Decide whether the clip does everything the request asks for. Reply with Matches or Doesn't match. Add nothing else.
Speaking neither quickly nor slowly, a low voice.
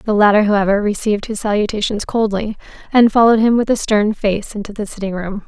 Doesn't match